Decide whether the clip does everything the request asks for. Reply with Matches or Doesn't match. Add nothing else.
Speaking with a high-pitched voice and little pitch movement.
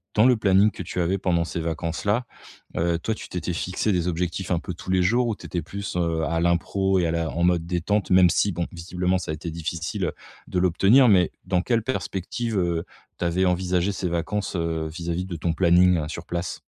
Doesn't match